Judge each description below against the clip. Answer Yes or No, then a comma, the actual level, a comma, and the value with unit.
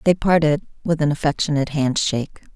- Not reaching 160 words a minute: Yes, average, 140 wpm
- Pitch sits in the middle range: Yes, medium, 155 Hz